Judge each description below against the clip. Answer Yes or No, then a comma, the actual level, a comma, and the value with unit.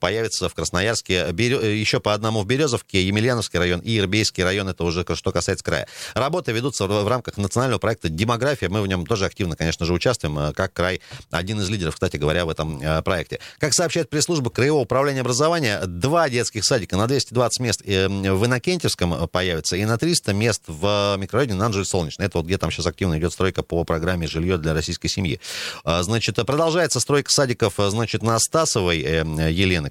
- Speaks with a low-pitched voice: Yes, low, 100 Hz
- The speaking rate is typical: No, fast, 175 wpm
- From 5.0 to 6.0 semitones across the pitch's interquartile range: Yes, wide, 5.4 semitones